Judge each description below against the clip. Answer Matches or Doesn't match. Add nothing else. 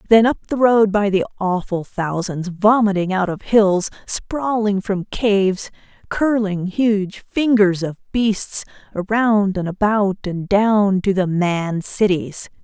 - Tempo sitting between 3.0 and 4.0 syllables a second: Matches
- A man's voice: Doesn't match